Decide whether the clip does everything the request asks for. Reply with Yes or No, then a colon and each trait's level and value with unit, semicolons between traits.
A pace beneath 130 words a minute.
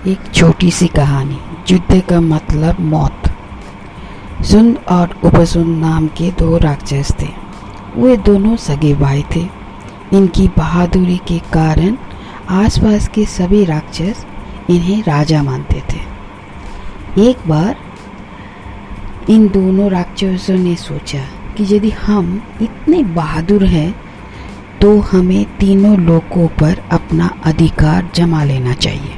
Yes: average, 115 wpm